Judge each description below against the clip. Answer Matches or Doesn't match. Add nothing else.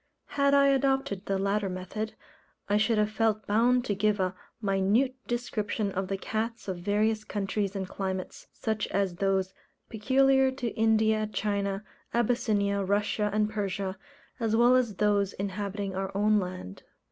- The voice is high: Matches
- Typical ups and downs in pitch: Doesn't match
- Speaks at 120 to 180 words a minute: Matches